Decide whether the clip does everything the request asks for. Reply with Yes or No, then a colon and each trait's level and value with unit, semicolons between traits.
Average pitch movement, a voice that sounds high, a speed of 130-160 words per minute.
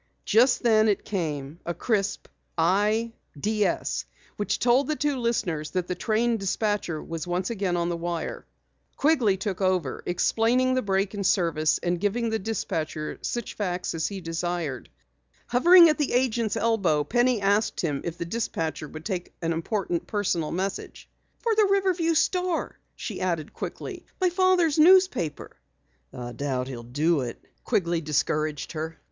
No: wide, 6.1 semitones; high, 195 Hz; average, 155 wpm